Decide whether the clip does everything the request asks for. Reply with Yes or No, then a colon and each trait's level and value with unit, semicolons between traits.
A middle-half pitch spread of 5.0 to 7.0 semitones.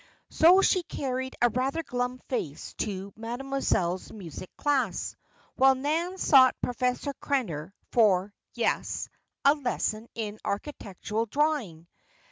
Yes: average, 5.3 semitones